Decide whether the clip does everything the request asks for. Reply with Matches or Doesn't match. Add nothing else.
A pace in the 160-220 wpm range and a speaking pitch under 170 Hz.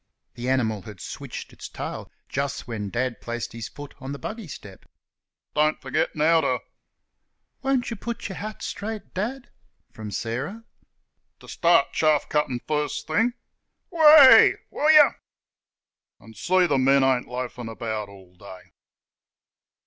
Doesn't match